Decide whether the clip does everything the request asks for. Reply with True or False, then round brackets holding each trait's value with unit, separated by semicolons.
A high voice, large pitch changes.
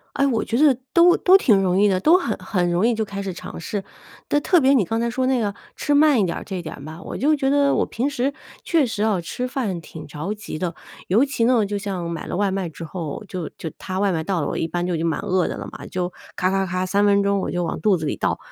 True (200 Hz; 5.9 semitones)